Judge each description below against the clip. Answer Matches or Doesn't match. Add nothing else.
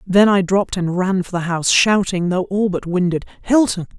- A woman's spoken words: Matches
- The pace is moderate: Matches